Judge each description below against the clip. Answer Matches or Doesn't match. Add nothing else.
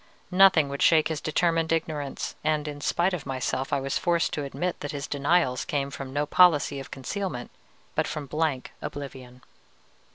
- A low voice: Doesn't match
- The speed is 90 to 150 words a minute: Doesn't match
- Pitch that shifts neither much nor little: Matches